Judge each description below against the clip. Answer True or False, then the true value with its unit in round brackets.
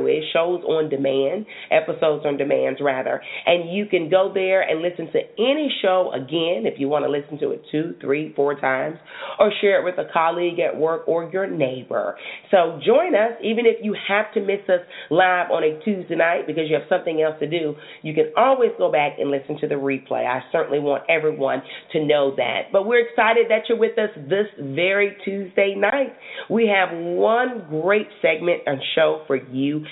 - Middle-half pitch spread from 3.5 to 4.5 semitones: False (5.2 semitones)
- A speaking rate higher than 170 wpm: True (200 wpm)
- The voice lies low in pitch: False (170 Hz)